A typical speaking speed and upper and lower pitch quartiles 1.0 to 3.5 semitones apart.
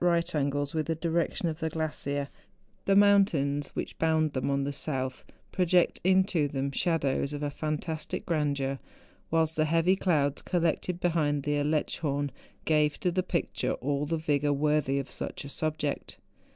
Yes: average, 160 wpm; average, 2.7 semitones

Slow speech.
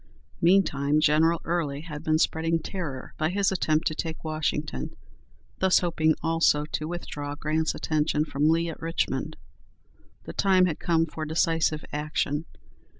No: average, 145 wpm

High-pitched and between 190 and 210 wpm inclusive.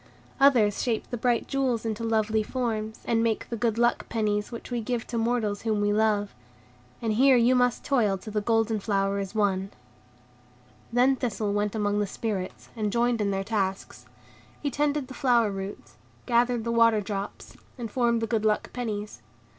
No: high, 225 Hz; average, 180 wpm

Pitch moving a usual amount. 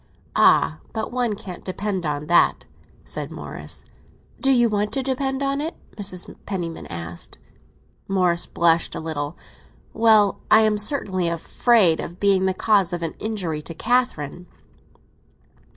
Yes: average, 4.8 semitones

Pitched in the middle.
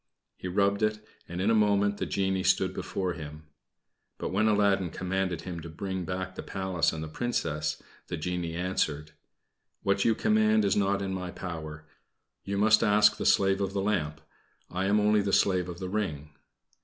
No: very low, 95 Hz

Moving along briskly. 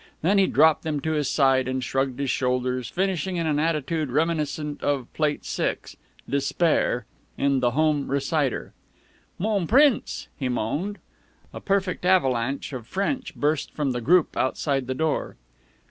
No: average, 150 wpm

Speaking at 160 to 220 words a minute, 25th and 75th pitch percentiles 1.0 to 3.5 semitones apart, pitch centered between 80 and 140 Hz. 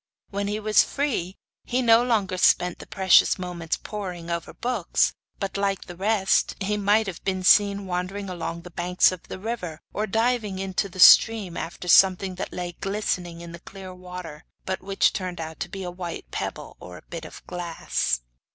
No: average, 190 wpm; narrow, 2.5 semitones; medium, 185 Hz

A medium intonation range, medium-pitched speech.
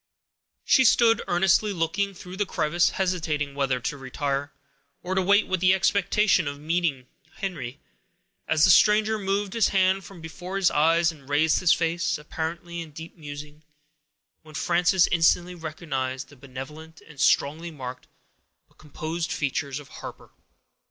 Yes: average, 4.2 semitones; medium, 165 Hz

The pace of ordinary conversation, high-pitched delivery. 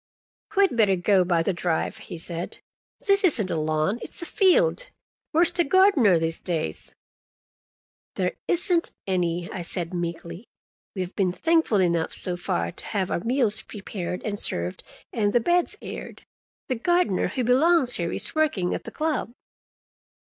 Yes: average, 160 wpm; high, 200 Hz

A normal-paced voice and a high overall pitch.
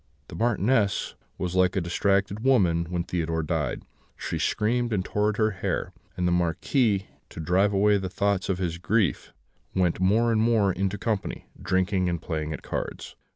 No: average, 170 wpm; very low, 95 Hz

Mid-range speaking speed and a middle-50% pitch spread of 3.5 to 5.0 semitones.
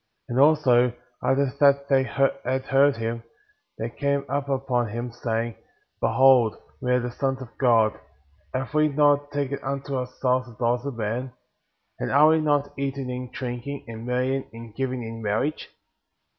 No: average, 160 wpm; narrow, 2.6 semitones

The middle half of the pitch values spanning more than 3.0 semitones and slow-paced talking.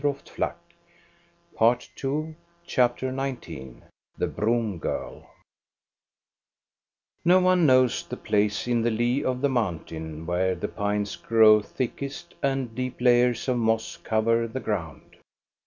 Yes: average, 3.9 semitones; slow, 125 wpm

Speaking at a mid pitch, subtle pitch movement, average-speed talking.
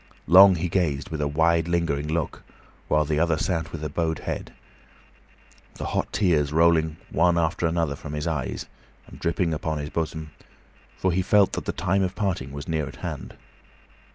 No: very low, 80 Hz; narrow, 2.2 semitones; average, 180 wpm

